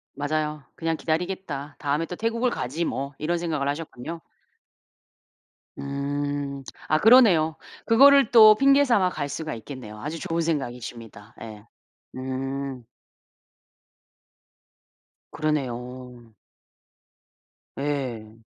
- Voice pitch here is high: No, medium, 145 Hz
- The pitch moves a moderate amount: Yes, average, 4.4 semitones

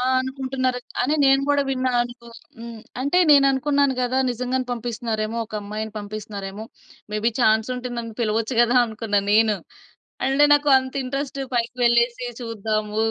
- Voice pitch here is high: Yes, high, 240 Hz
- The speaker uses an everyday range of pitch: Yes, average, 3.0 semitones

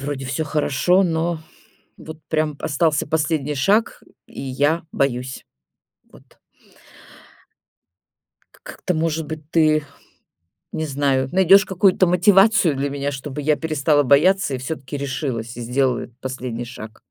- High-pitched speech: No, medium, 150 Hz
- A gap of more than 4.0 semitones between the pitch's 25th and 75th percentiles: No, average, 3.3 semitones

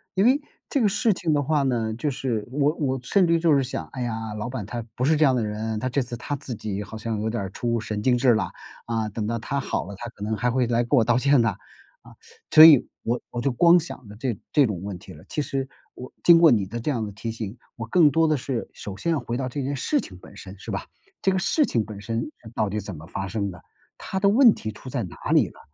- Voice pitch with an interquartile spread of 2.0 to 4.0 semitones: No, average, 4.8 semitones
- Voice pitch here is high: No, low, 120 Hz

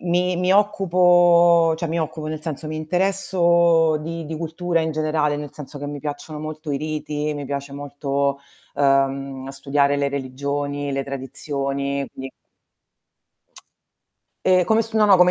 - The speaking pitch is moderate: Yes, medium, 155 Hz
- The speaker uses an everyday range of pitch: Yes, average, 3.3 semitones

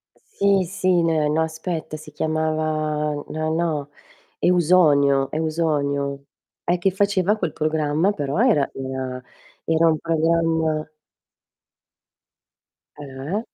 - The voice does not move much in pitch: Yes, narrow, 2.3 semitones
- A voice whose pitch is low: No, medium, 155 Hz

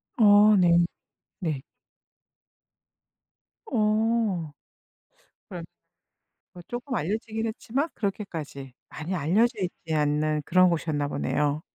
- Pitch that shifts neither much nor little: No, wide, 6.1 semitones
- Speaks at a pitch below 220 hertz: Yes, medium, 185 Hz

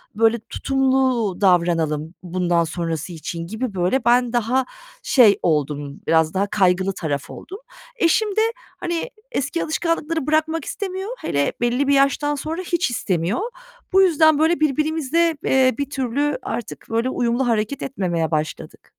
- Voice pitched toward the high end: Yes, high, 245 Hz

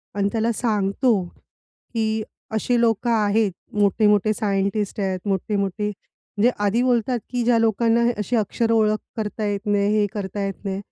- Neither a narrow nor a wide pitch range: No, narrow, 2.2 semitones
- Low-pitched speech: No, high, 210 Hz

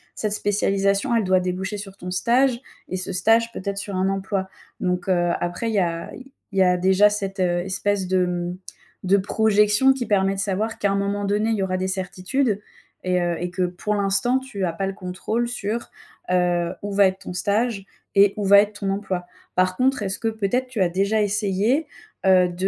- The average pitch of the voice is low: No, high, 195 Hz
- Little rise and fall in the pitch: Yes, narrow, 2.2 semitones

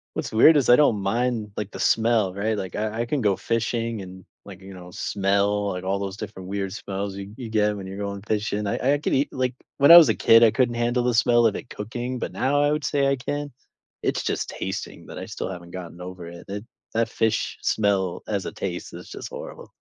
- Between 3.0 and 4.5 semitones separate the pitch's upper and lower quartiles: Yes, average, 3.6 semitones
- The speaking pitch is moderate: No, low, 105 Hz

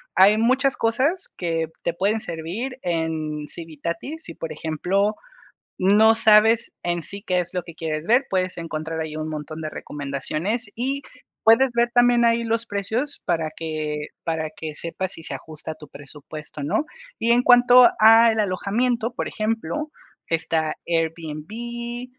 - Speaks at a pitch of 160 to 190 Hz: Yes, medium, 185 Hz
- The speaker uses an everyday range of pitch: No, wide, 6.5 semitones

